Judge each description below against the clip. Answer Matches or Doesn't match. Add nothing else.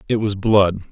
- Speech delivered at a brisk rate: Doesn't match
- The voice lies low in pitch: Matches